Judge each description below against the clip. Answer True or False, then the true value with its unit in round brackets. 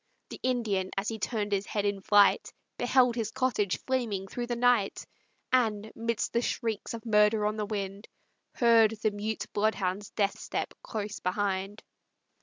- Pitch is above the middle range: True (215 Hz)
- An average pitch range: False (2.3 semitones)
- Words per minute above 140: True (160 wpm)